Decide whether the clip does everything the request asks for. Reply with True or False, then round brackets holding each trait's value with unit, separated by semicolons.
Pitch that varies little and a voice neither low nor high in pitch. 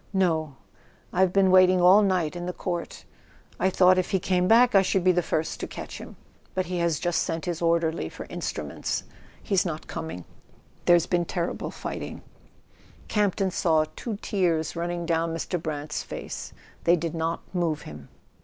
True (2.2 semitones; 175 Hz)